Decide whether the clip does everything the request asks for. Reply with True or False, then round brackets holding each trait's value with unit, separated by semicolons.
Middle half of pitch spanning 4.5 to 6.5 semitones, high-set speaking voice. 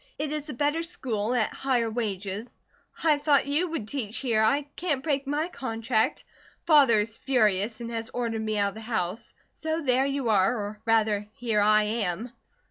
True (4.8 semitones; 230 Hz)